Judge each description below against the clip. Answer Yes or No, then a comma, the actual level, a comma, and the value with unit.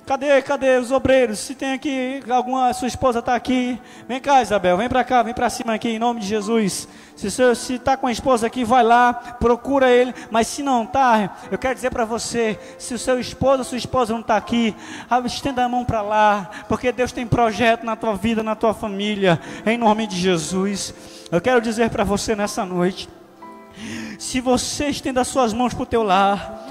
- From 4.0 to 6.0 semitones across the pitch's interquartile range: No, narrow, 2.5 semitones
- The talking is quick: Yes, fast, 205 wpm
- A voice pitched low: No, high, 240 Hz